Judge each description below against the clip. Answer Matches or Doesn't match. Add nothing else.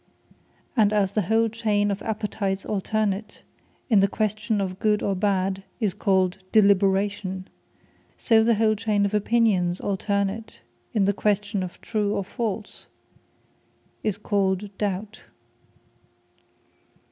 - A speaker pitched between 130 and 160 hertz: Doesn't match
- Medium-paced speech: Doesn't match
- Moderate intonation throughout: Doesn't match